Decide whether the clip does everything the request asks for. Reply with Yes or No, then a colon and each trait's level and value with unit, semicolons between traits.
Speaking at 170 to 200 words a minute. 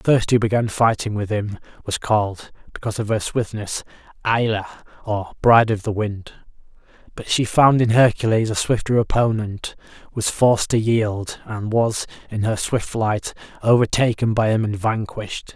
No: average, 160 wpm